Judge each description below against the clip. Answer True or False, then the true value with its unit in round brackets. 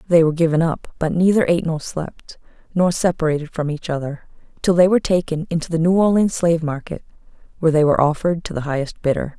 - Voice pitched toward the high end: False (165 Hz)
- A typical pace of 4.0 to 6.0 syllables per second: False (6.6 syllables/s)